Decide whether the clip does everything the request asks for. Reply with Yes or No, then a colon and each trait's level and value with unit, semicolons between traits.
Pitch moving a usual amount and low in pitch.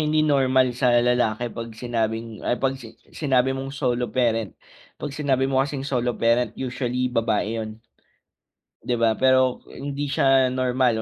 No: narrow, 2.3 semitones; low, 125 Hz